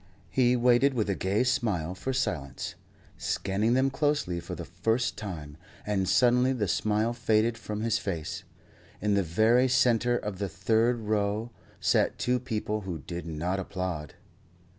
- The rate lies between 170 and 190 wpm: No, average, 155 wpm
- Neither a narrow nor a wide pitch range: Yes, average, 4.4 semitones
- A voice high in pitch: No, low, 110 Hz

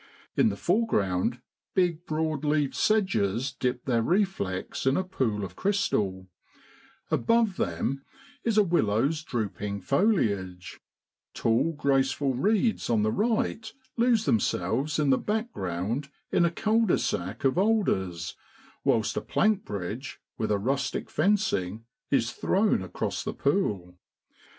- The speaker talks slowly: Yes, slow, 125 wpm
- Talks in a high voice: No, low, 135 Hz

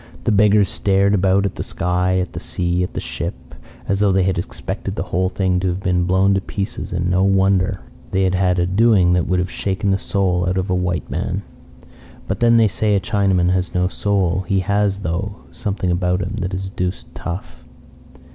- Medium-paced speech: No, fast, 215 wpm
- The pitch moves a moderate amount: No, narrow, 1.5 semitones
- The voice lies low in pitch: Yes, very low, 95 Hz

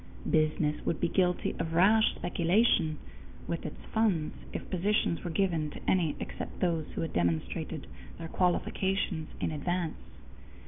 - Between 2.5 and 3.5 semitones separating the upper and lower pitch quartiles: Yes, average, 3.1 semitones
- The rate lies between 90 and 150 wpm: Yes, average, 140 wpm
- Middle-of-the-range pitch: Yes, medium, 170 Hz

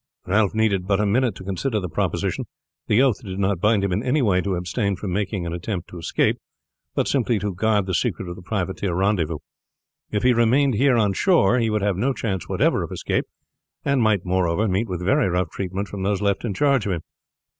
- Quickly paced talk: Yes, fast, 220 wpm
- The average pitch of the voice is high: No, low, 100 Hz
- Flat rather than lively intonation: No, average, 3.3 semitones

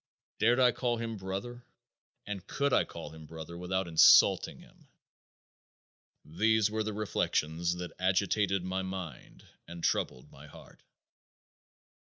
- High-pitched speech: No, very low, 95 Hz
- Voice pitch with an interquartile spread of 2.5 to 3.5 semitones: No, average, 4.2 semitones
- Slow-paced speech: Yes, slow, 130 wpm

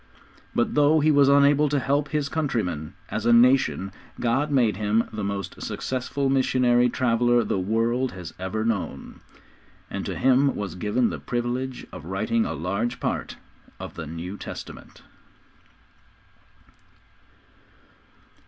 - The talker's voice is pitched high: No, low, 120 Hz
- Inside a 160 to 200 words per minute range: No, slow, 135 wpm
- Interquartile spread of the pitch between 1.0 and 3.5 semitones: No, average, 4.7 semitones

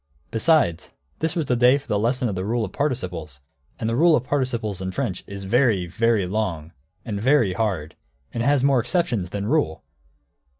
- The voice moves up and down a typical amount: No, wide, 5.7 semitones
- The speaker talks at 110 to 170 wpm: No, average, 195 wpm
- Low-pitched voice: Yes, low, 115 Hz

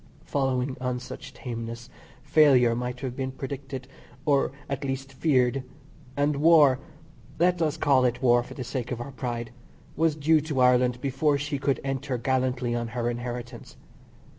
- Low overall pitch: Yes, low, 130 Hz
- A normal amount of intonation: No, narrow, 2.3 semitones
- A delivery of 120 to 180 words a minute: Yes, average, 160 wpm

